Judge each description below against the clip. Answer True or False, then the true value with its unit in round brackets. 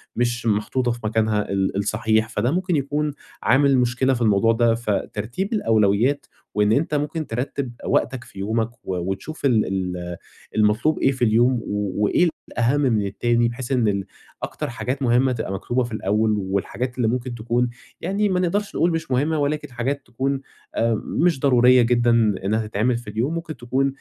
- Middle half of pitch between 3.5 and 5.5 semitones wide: True (4.0 semitones)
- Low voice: True (120 Hz)